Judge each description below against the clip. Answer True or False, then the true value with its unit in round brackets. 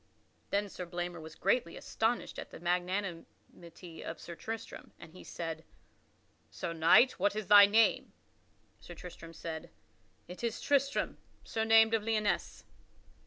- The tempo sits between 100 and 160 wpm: True (135 wpm)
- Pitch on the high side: False (180 Hz)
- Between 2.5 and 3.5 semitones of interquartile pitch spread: False (4.7 semitones)